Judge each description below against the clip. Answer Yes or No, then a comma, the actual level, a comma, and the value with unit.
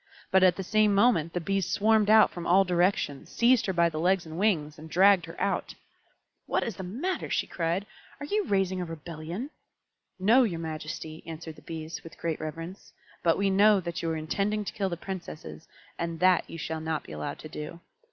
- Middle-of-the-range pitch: Yes, medium, 175 Hz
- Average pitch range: Yes, average, 3.6 semitones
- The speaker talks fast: Yes, fast, 210 wpm